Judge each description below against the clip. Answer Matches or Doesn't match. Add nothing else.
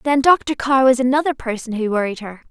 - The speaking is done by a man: Doesn't match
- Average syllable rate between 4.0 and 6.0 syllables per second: Matches